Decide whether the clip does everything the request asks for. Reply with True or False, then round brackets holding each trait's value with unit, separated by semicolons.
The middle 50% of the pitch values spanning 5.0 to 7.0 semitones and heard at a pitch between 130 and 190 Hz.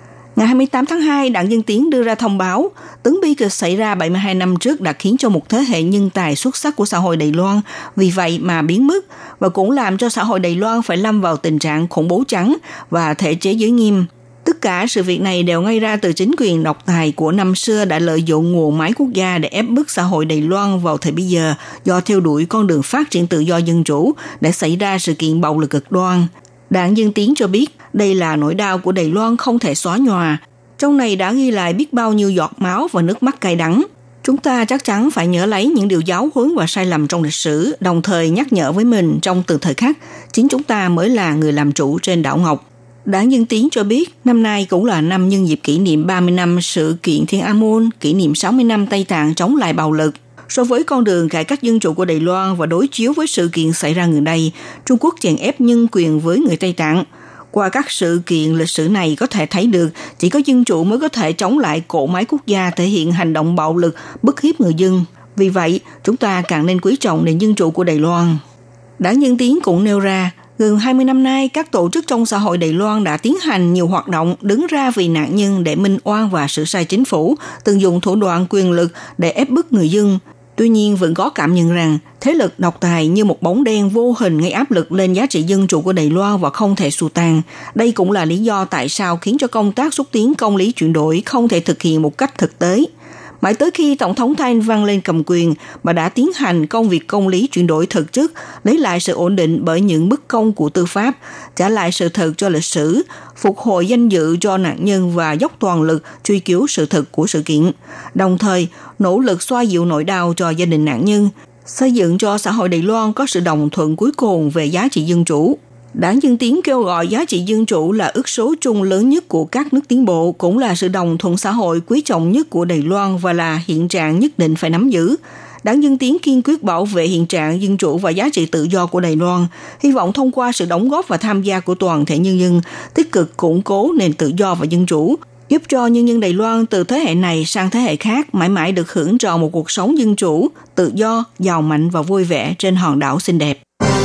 True (5.4 semitones; 185 Hz)